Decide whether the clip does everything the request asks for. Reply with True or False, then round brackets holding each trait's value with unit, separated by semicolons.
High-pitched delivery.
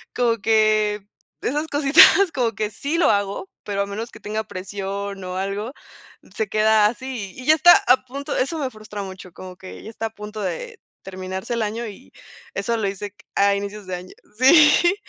True (215 Hz)